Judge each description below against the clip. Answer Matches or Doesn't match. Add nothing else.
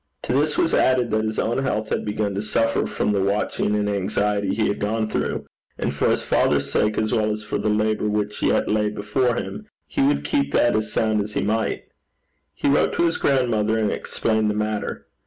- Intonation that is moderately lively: Doesn't match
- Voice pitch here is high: Doesn't match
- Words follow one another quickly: Matches